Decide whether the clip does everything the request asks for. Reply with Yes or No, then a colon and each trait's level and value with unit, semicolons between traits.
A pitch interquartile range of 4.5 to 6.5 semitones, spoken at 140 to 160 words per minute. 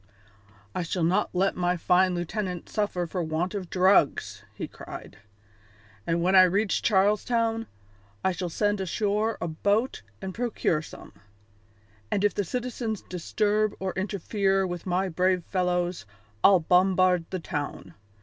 No: narrow, 2.6 semitones; average, 145 wpm